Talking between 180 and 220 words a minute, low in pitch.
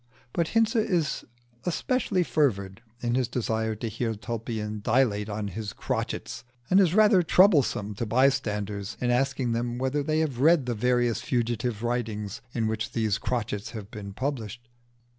No: average, 155 wpm; low, 120 Hz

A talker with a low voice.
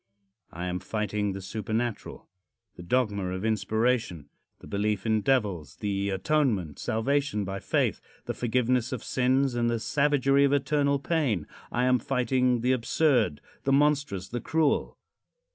Yes: low, 120 Hz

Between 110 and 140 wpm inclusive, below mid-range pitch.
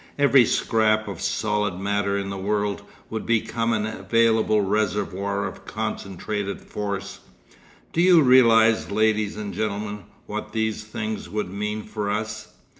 Yes: slow, 135 wpm; low, 105 Hz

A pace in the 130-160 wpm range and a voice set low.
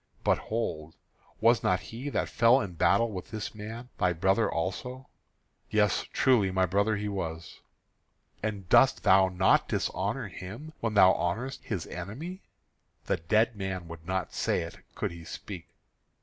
Yes: average, 155 wpm; low, 100 Hz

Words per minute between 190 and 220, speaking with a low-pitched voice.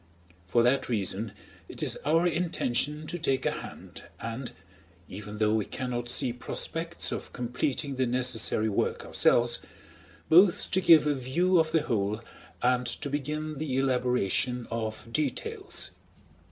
No: average, 140 wpm; low, 125 Hz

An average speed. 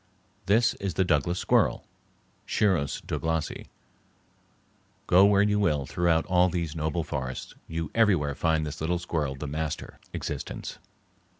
No: slow, 130 wpm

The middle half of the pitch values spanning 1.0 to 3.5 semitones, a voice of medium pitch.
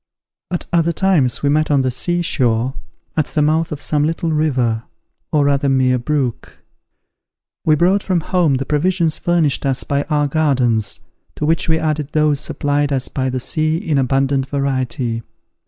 Yes: average, 3.1 semitones; medium, 145 Hz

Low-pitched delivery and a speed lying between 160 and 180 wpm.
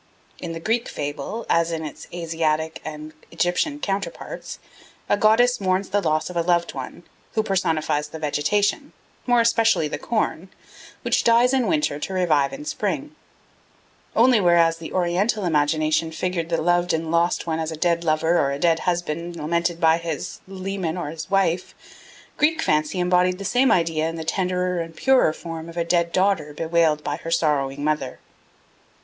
No: medium, 170 Hz; average, 170 wpm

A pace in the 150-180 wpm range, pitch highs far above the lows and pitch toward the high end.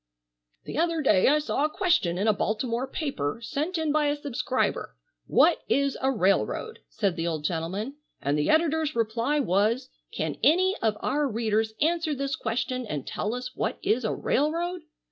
Yes: average, 175 wpm; wide, 6.0 semitones; very high, 255 Hz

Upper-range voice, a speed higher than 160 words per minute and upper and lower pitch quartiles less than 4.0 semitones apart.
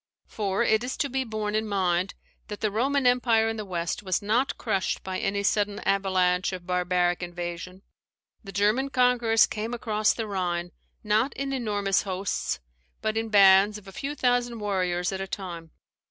Yes: high, 205 Hz; average, 175 wpm; average, 3.3 semitones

